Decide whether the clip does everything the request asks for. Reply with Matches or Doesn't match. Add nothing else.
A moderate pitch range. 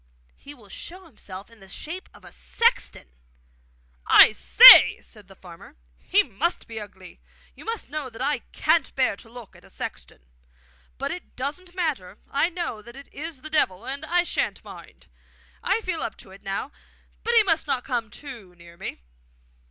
Doesn't match